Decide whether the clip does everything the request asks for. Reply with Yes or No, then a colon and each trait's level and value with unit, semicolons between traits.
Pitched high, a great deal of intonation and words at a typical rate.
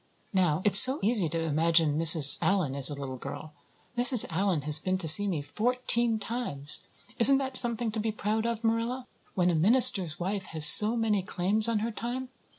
Yes: high, 200 Hz; wide, 6.3 semitones; average, 190 wpm